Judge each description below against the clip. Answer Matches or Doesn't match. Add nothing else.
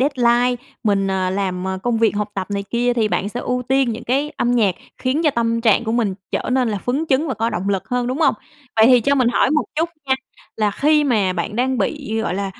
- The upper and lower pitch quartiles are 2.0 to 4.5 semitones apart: Matches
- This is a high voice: Matches